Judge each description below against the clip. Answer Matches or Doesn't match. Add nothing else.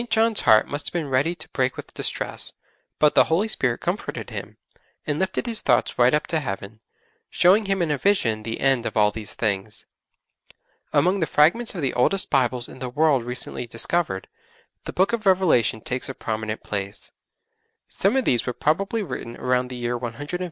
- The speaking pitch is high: Doesn't match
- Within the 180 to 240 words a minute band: Matches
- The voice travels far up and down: Matches